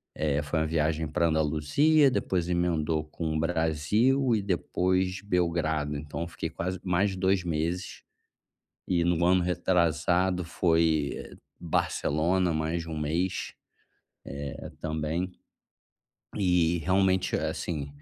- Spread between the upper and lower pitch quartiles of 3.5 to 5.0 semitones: No, average, 2.9 semitones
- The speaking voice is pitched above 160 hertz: No, very low, 85 Hz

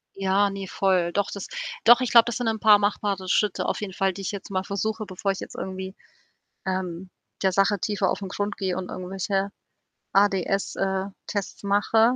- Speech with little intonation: Yes, narrow, 1.5 semitones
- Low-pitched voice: No, high, 195 Hz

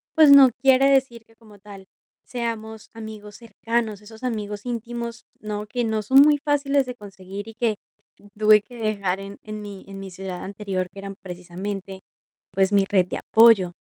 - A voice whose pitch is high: Yes, high, 215 Hz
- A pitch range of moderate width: Yes, average, 3.1 semitones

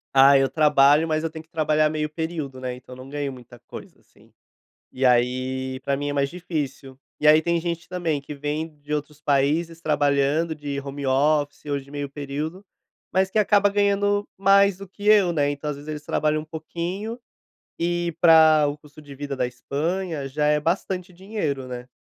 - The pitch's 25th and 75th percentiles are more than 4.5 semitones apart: No, average, 3.4 semitones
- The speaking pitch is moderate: Yes, medium, 150 Hz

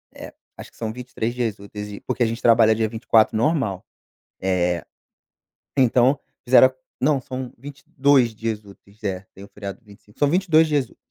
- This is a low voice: Yes, low, 115 Hz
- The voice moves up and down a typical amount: Yes, average, 4.1 semitones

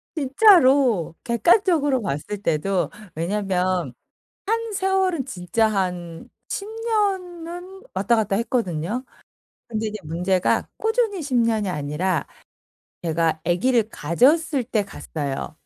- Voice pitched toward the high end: Yes, high, 220 Hz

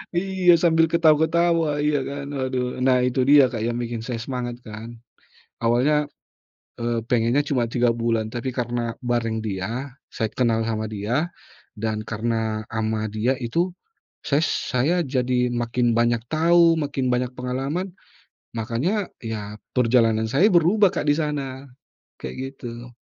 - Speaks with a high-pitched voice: No, low, 125 Hz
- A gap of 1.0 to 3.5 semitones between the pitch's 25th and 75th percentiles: No, average, 4.1 semitones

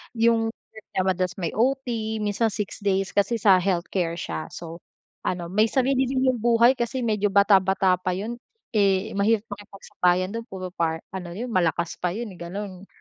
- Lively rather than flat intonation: No, average, 3.6 semitones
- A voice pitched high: Yes, high, 200 Hz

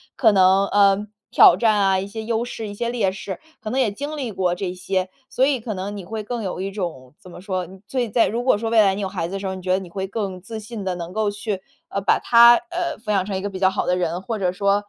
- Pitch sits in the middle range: No, high, 200 Hz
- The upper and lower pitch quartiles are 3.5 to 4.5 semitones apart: No, average, 2.9 semitones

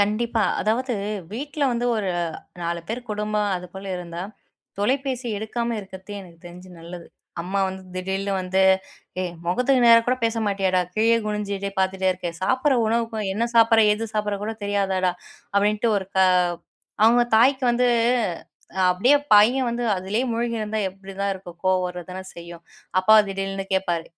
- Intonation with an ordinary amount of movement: Yes, average, 3.5 semitones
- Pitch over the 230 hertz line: No, high, 205 Hz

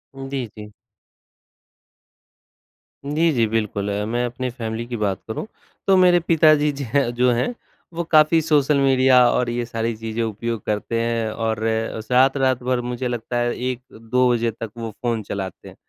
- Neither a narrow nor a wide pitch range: Yes, average, 3.0 semitones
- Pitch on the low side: Yes, low, 120 Hz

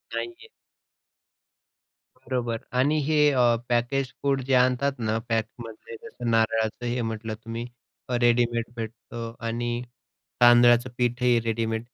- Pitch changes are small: Yes, narrow, 1.6 semitones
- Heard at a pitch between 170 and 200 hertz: No, low, 120 Hz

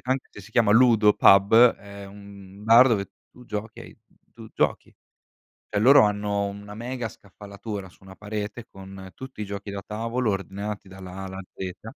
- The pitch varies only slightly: Yes, narrow, 2.1 semitones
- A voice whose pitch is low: Yes, low, 105 Hz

